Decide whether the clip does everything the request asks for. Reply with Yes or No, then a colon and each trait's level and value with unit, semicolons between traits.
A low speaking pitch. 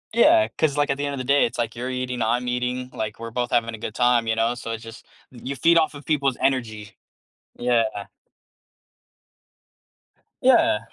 Yes: low, 125 Hz